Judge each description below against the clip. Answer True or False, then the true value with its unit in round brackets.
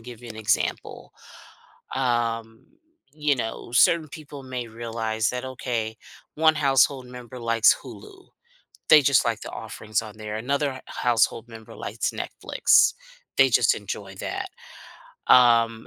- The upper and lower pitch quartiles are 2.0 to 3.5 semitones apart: True (3.1 semitones)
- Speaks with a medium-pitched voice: False (120 Hz)